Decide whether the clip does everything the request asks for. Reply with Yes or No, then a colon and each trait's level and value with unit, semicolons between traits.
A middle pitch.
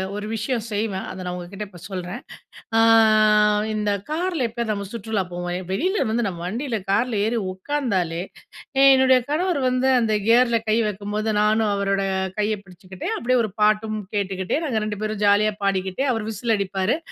No: high, 215 Hz